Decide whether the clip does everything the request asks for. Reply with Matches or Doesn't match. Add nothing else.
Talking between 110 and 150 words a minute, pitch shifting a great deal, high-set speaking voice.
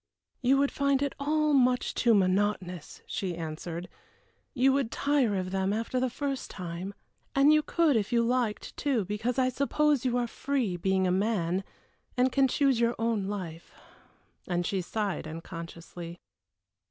Doesn't match